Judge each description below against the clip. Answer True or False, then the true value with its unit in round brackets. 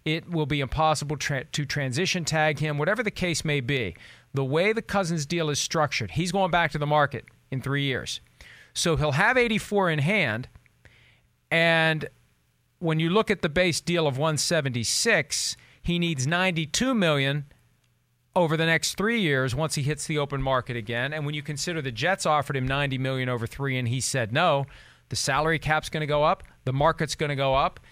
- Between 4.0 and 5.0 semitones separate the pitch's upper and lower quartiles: False (3.4 semitones)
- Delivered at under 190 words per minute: False (195 wpm)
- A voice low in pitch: False (150 Hz)